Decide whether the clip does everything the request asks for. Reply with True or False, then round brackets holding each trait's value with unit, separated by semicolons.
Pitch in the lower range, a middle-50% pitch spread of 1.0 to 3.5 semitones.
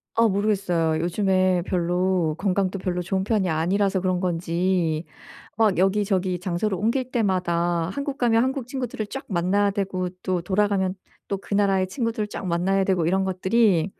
False (190 Hz; 2.5 semitones)